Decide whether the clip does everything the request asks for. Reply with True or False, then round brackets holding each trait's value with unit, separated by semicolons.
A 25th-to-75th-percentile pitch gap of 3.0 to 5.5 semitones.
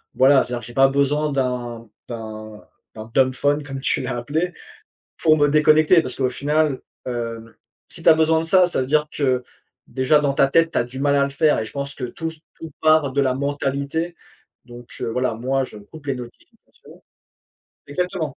True (3.5 semitones)